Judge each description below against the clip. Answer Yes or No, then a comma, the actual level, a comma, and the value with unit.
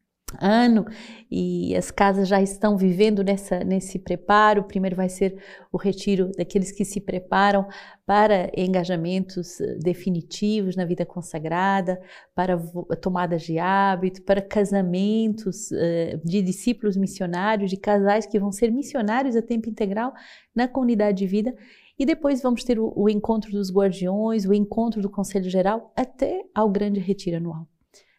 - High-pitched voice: Yes, high, 200 Hz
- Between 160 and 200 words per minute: No, average, 145 wpm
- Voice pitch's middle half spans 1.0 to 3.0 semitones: Yes, narrow, 2.5 semitones